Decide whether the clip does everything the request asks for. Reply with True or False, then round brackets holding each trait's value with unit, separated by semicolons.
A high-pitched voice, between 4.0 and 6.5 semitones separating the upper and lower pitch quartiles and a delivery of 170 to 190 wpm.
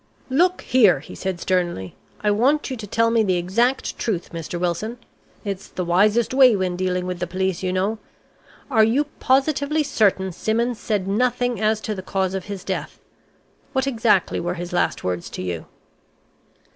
True (205 Hz; 4.7 semitones; 175 wpm)